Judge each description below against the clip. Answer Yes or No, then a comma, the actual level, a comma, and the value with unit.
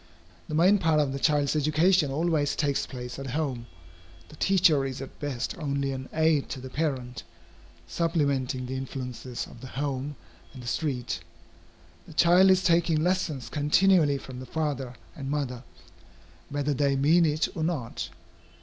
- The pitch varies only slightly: No, average, 3.4 semitones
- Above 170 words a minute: No, average, 160 wpm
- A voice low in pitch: No, medium, 145 Hz